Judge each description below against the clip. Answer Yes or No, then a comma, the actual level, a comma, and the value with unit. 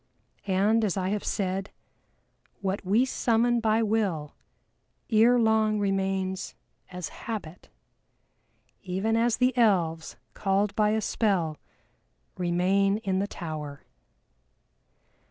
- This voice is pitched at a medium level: No, high, 200 Hz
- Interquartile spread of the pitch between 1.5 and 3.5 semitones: Yes, average, 3.0 semitones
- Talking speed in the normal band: No, slow, 105 wpm